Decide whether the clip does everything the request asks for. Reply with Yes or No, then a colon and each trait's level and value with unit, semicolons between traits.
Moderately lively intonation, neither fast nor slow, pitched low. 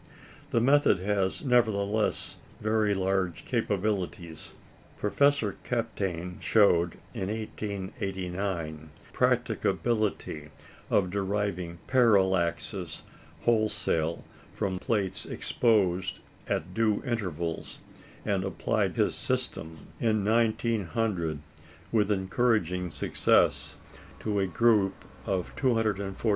No: average, 3.3 semitones; slow, 90 wpm; low, 100 Hz